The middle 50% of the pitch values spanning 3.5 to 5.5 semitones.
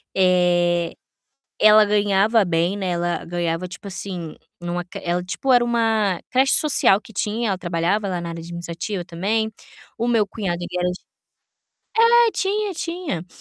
Yes: average, 3.9 semitones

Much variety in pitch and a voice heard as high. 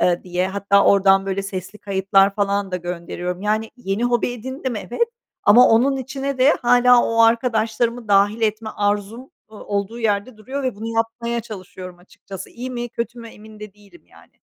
No: average, 3.4 semitones; high, 215 Hz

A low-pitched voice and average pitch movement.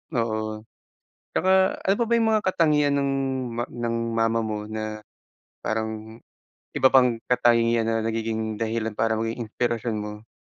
No: low, 115 Hz; narrow, 1.8 semitones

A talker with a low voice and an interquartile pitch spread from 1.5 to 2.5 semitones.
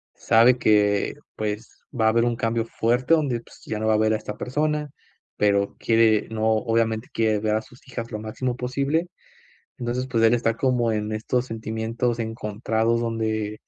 Yes: low, 115 Hz; narrow, 1.9 semitones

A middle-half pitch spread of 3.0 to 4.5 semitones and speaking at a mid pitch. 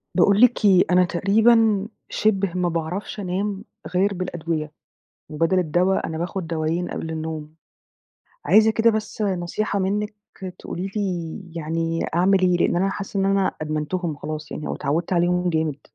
Yes: average, 3.3 semitones; medium, 180 Hz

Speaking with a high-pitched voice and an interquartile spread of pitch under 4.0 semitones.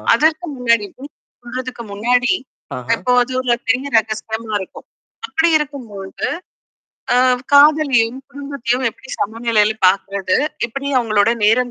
Yes: high, 240 Hz; average, 3.5 semitones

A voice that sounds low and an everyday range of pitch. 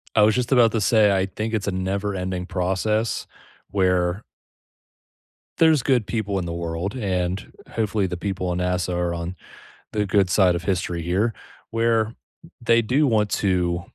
Yes: very low, 95 Hz; average, 3.5 semitones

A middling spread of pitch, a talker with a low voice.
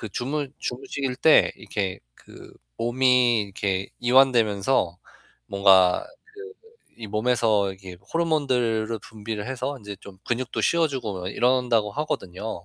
Yes: average, 4.6 semitones; low, 115 Hz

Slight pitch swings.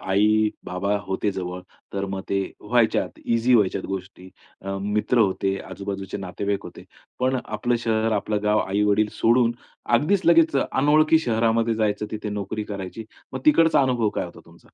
No: average, 3.2 semitones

